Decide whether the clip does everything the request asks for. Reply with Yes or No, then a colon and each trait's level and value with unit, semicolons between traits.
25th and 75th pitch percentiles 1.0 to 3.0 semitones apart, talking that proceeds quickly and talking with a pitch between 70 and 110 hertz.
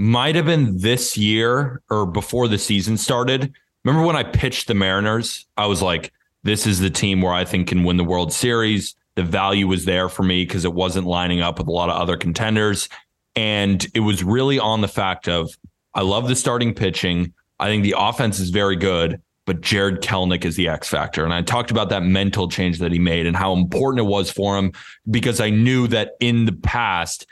No: average, 4.0 semitones; fast, 215 wpm; low, 100 Hz